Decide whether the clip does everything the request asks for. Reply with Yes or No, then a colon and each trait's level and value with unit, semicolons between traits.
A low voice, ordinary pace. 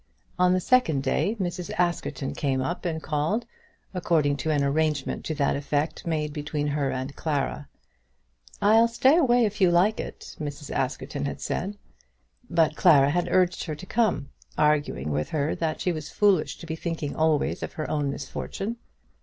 No: medium, 155 Hz; average, 170 wpm